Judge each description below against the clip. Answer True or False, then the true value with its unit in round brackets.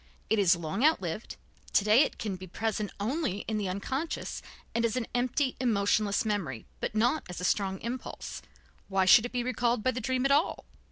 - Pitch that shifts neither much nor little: True (4.3 semitones)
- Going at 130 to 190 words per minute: False (200 wpm)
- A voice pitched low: False (220 Hz)